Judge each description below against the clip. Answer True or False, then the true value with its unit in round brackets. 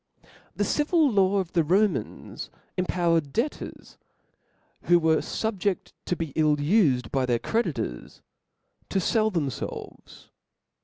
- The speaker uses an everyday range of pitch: False (5.7 semitones)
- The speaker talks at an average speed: False (115 wpm)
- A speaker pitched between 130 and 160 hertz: False (175 Hz)